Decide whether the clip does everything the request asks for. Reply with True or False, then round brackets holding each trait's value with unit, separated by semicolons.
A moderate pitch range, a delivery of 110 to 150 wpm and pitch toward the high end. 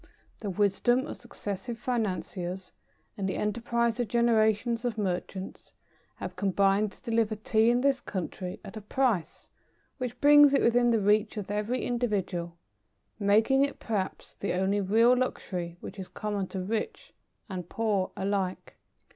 True (3.6 semitones; 145 wpm; 210 Hz)